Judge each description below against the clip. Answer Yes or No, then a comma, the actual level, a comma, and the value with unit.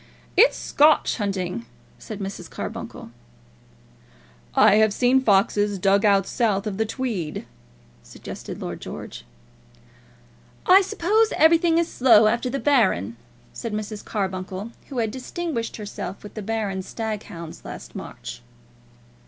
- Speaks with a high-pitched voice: Yes, high, 215 Hz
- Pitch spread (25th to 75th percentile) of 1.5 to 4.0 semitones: No, average, 4.9 semitones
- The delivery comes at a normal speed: No, slow, 130 wpm